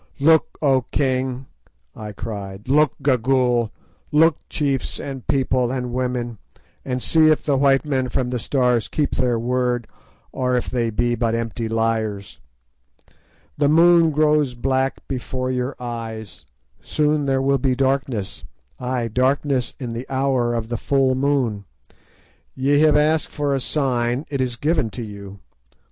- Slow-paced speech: No, average, 145 wpm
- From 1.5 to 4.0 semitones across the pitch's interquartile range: Yes, average, 2.7 semitones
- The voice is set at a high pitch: No, low, 130 Hz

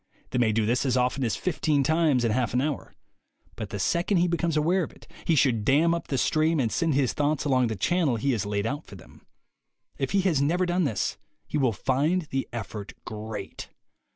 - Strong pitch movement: Yes, wide, 5.8 semitones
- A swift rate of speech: Yes, fast, 220 wpm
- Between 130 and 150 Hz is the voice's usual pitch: Yes, low, 135 Hz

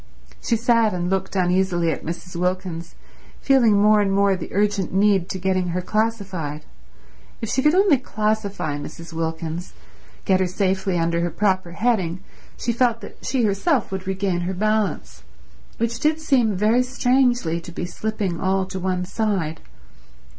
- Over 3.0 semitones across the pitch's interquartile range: Yes, average, 3.6 semitones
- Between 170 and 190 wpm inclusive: No, average, 160 wpm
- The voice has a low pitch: No, high, 190 Hz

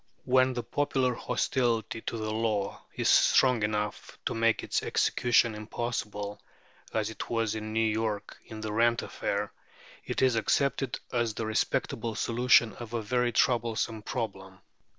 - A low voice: Yes, low, 115 Hz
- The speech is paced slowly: No, average, 150 wpm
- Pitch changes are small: Yes, narrow, 2.0 semitones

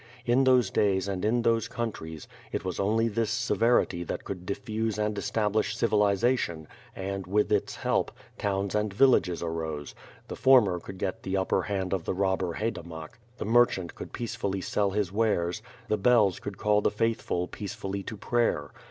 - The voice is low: Yes, low, 100 Hz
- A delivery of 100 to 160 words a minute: No, average, 170 wpm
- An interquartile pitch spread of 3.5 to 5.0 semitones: No, average, 3.1 semitones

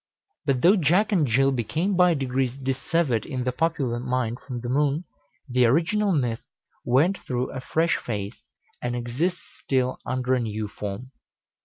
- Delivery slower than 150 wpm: No, average, 160 wpm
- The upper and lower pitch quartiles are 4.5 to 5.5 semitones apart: Yes, average, 4.9 semitones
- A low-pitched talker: Yes, low, 130 Hz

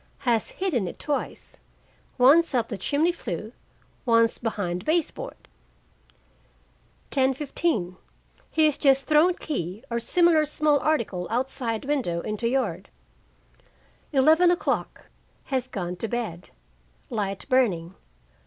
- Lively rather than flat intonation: Yes, wide, 6.5 semitones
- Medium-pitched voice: No, very high, 255 Hz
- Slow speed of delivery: Yes, slow, 110 wpm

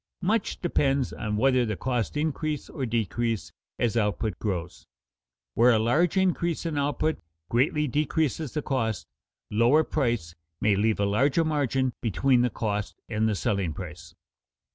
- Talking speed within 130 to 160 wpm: Yes, average, 145 wpm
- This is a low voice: Yes, low, 120 Hz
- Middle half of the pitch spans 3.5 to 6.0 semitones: Yes, wide, 5.6 semitones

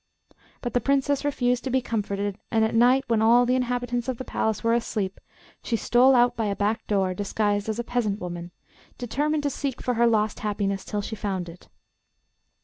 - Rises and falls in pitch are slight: No, average, 3.2 semitones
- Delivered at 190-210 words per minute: Yes, average, 200 wpm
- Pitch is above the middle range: Yes, high, 230 Hz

